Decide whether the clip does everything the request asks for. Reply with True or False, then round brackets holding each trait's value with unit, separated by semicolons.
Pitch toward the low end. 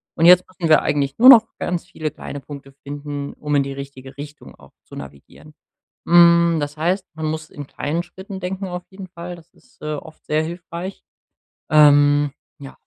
False (155 Hz)